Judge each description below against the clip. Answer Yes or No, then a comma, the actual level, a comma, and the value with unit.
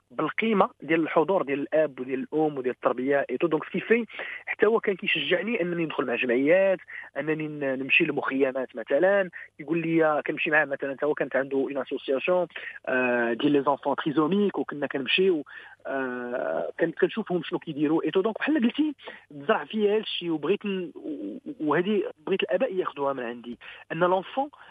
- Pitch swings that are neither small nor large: No, wide, 6.9 semitones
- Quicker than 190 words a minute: No, average, 145 wpm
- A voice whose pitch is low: No, medium, 165 Hz